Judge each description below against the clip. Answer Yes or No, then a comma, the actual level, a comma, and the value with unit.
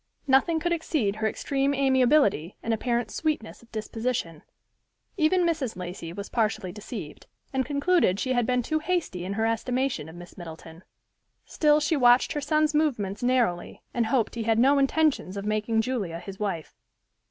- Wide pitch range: Yes, wide, 6.0 semitones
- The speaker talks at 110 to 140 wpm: No, average, 165 wpm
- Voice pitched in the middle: No, high, 240 Hz